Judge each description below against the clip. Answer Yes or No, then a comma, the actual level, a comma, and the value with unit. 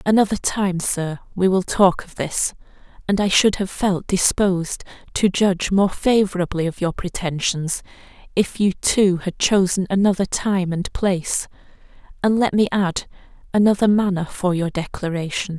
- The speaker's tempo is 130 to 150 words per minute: Yes, average, 140 wpm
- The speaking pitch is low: No, high, 190 Hz